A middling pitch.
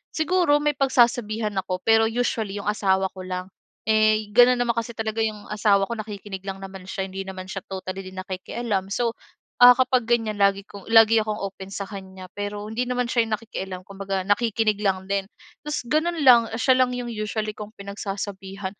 No: high, 210 Hz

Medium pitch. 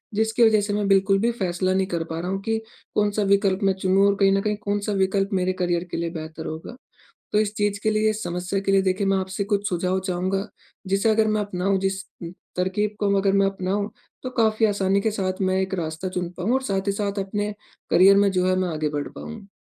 No: high, 195 Hz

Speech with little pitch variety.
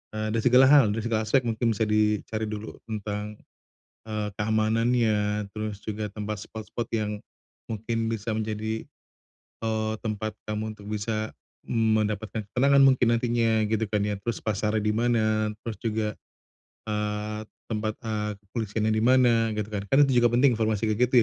Yes: narrow, 1.2 semitones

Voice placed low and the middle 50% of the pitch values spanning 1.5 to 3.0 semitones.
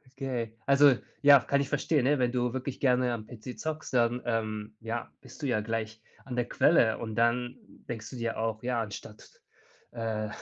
Yes: low, 120 Hz; narrow, 2.6 semitones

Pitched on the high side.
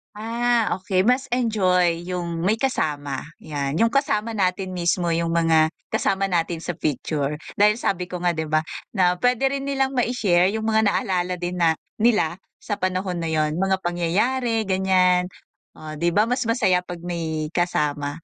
No: medium, 180 Hz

